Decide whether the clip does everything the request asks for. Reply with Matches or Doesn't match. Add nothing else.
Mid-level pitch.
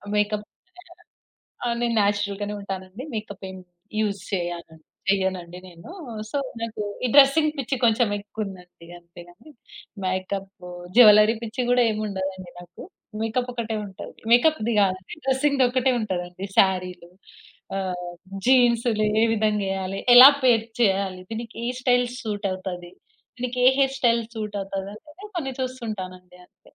Doesn't match